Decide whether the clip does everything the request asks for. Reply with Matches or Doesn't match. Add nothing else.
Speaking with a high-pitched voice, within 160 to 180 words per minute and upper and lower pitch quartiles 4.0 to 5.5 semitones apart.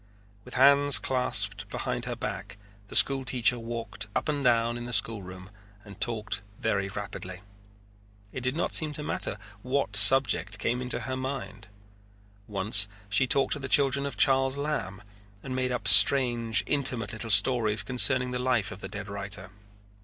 Doesn't match